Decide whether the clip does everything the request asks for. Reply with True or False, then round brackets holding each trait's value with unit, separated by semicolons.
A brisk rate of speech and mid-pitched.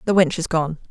True (265 wpm; 170 Hz)